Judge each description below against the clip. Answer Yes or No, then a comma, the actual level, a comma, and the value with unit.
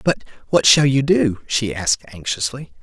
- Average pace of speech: Yes, average, 150 wpm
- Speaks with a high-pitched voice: No, low, 125 Hz